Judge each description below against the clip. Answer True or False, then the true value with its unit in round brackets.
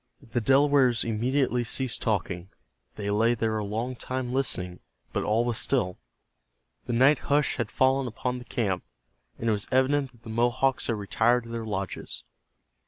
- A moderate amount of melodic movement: True (3.2 semitones)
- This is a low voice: True (120 Hz)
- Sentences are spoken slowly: False (170 wpm)